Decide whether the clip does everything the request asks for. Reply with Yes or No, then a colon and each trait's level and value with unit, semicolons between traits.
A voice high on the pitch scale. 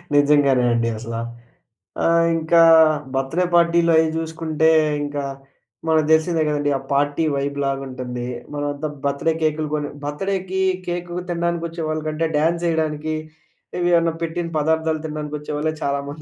No: medium, 155 Hz